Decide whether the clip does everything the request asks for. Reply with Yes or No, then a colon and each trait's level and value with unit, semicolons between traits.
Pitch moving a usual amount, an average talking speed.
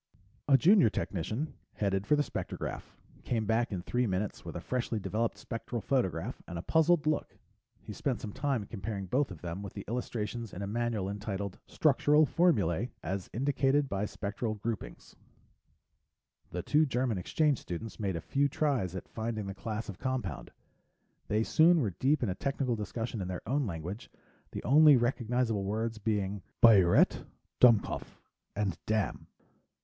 Yes: average, 4.9 semitones; average, 160 wpm